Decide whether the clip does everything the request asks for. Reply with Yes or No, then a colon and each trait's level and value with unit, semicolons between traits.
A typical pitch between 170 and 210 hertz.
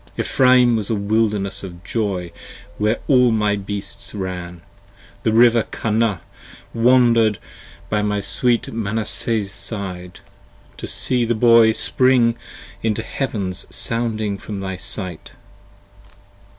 No: low, 110 Hz